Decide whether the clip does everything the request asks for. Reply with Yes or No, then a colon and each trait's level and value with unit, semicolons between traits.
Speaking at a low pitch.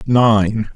Yes: low, 110 Hz